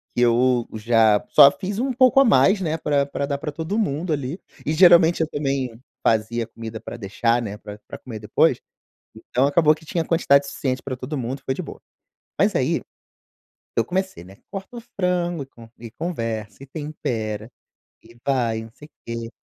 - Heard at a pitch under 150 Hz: Yes, medium, 140 Hz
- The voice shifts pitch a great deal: Yes, wide, 6.0 semitones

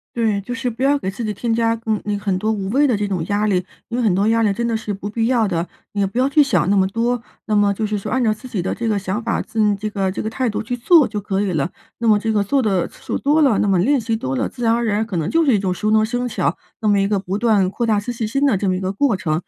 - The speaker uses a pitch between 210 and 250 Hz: Yes, high, 215 Hz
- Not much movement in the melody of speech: No, average, 3.1 semitones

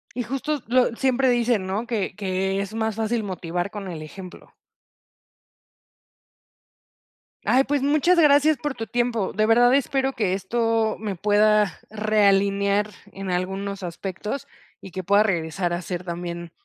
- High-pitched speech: Yes, high, 210 Hz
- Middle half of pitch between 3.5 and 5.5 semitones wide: Yes, average, 4.2 semitones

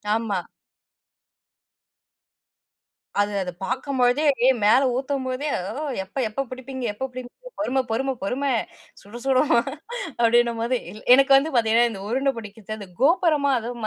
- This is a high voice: Yes, very high, 255 Hz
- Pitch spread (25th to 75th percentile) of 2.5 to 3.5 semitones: Yes, average, 3.2 semitones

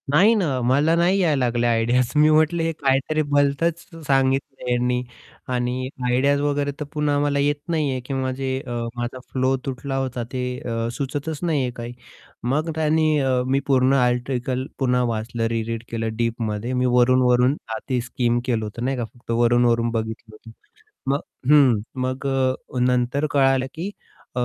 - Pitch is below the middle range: Yes, low, 130 Hz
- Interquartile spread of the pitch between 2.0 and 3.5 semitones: Yes, average, 2.8 semitones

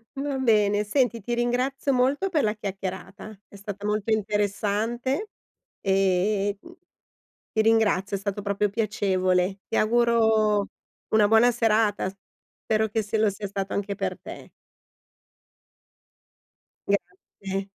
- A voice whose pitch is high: Yes, high, 210 Hz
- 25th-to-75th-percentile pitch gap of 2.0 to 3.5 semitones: Yes, narrow, 2.5 semitones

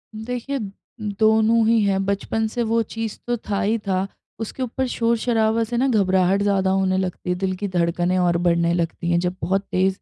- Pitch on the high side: Yes, high, 200 Hz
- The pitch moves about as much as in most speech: Yes, average, 3.5 semitones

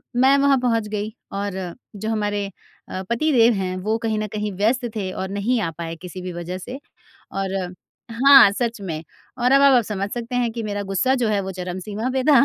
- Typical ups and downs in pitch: Yes, average, 4.0 semitones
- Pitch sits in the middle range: No, high, 215 Hz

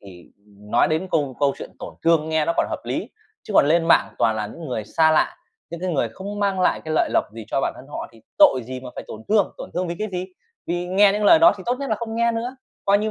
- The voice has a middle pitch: Yes, medium, 170 Hz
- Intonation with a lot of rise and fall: Yes, wide, 7.7 semitones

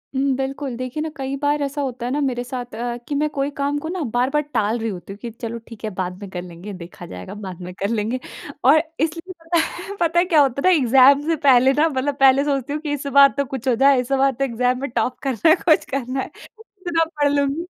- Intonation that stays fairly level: No, average, 3.4 semitones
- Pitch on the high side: Yes, very high, 270 Hz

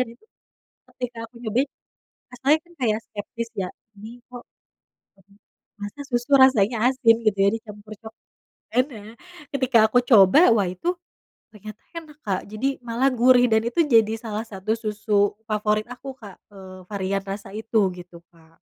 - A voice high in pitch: Yes, high, 220 Hz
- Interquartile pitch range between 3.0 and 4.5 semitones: Yes, average, 3.3 semitones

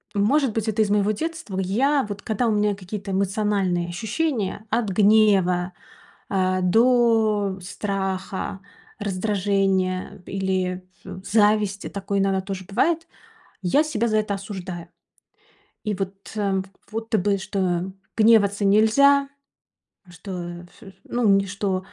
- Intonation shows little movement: Yes, narrow, 2.3 semitones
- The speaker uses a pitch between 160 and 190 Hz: No, high, 200 Hz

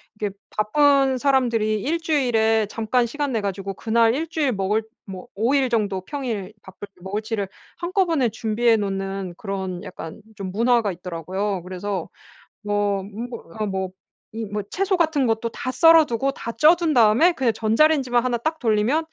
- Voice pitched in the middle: No, high, 225 Hz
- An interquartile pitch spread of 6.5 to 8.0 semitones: No, average, 5.1 semitones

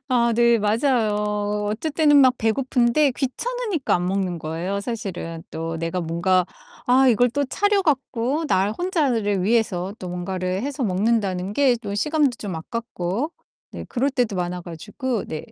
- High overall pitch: Yes, high, 220 Hz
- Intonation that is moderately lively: No, wide, 6.1 semitones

